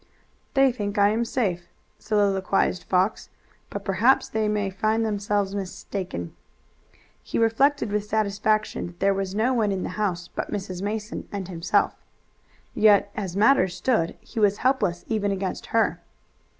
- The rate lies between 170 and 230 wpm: No, average, 150 wpm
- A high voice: Yes, high, 205 Hz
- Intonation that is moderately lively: No, narrow, 2.3 semitones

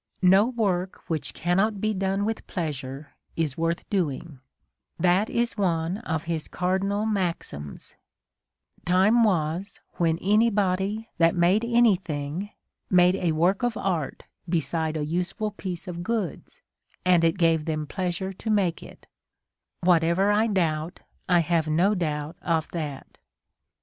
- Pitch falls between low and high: Yes, medium, 180 Hz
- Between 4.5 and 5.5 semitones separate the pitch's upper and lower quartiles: No, average, 3.6 semitones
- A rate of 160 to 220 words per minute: No, average, 140 wpm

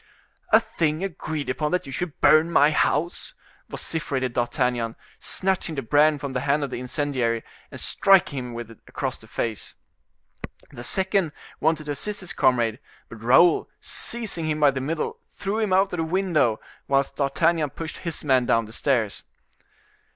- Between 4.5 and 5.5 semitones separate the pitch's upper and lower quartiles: Yes, average, 4.9 semitones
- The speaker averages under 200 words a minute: Yes, average, 170 wpm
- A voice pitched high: No, medium, 145 Hz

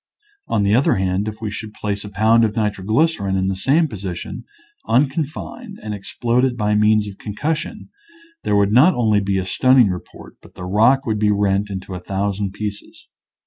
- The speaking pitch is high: No, low, 105 Hz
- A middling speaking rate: Yes, average, 185 wpm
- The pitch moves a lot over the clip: No, average, 3.4 semitones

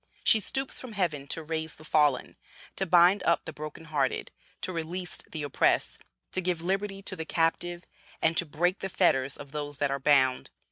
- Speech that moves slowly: No, average, 190 wpm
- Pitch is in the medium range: Yes, medium, 165 Hz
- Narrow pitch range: No, average, 3.7 semitones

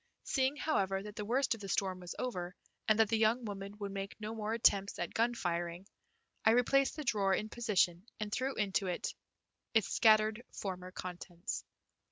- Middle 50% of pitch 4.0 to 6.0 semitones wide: No, average, 2.9 semitones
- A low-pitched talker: No, high, 210 Hz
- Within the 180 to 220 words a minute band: Yes, average, 185 wpm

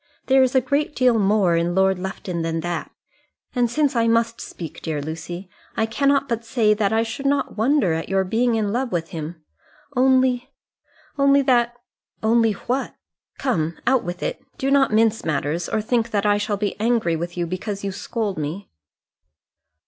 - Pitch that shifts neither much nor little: No, wide, 5.7 semitones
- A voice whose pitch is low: No, high, 220 Hz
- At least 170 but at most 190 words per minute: Yes, average, 185 wpm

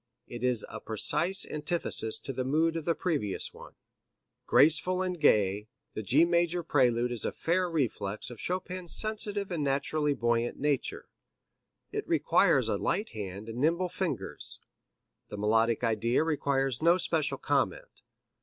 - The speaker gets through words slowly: No, average, 145 wpm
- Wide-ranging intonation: Yes, wide, 6.6 semitones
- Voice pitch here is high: No, medium, 145 Hz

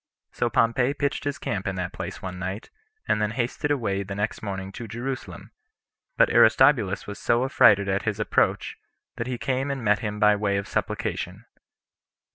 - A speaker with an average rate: Yes, average, 180 wpm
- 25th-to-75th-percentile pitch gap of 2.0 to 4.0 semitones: No, average, 4.5 semitones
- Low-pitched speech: Yes, low, 105 Hz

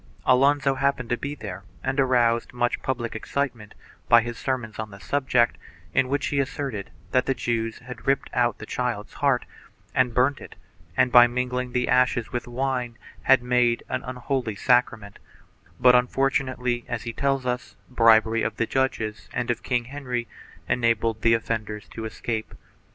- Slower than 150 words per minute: No, average, 165 wpm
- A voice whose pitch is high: No, low, 125 Hz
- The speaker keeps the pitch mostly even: Yes, narrow, 2.2 semitones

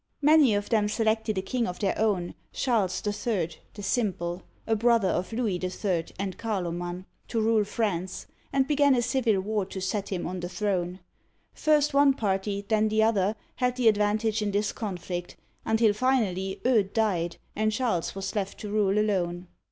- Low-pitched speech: No, high, 210 Hz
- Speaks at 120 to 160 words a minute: No, average, 175 wpm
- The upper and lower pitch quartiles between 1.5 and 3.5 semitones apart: Yes, average, 3.1 semitones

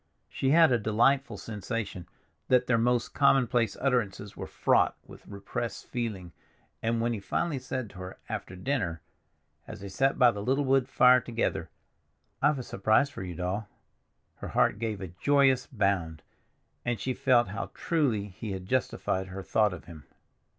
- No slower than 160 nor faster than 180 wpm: Yes, average, 165 wpm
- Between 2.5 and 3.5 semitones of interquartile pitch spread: No, average, 4.7 semitones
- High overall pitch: No, low, 115 Hz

